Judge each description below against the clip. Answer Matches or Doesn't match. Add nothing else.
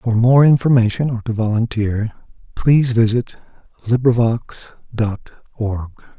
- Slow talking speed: Matches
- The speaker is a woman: Doesn't match